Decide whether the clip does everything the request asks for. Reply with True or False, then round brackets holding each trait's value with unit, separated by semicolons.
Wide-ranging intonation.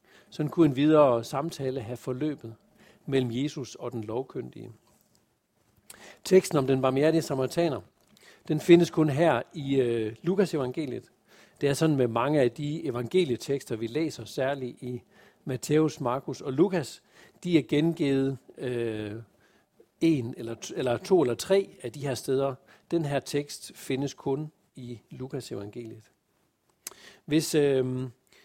False (4.0 semitones)